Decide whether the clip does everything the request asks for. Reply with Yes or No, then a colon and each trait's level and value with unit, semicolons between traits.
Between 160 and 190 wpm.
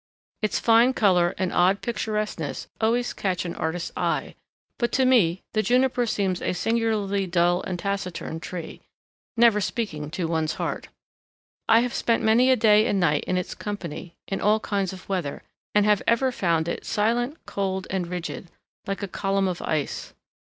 Yes: average, 170 wpm